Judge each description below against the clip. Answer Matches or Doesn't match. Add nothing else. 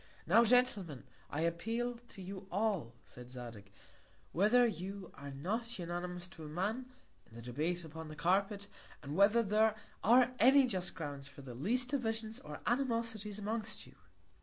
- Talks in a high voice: Matches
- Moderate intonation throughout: Doesn't match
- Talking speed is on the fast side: Doesn't match